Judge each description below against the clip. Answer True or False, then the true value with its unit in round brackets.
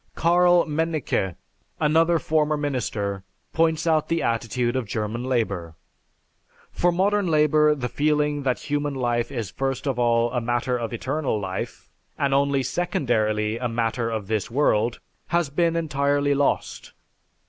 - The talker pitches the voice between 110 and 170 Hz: True (135 Hz)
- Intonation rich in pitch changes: False (4.7 semitones)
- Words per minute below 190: True (140 wpm)